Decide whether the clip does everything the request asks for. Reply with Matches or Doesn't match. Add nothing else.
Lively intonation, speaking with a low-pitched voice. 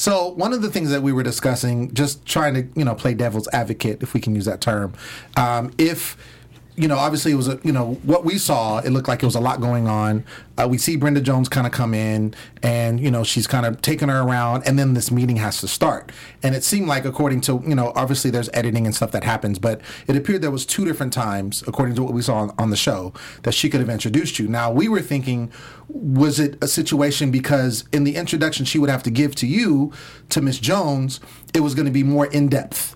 Doesn't match